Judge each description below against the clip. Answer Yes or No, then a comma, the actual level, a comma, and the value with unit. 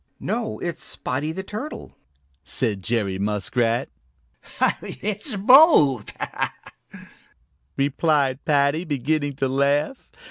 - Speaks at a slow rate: Yes, slow, 85 wpm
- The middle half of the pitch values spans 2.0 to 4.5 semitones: No, average, 5.2 semitones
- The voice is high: No, medium, 140 Hz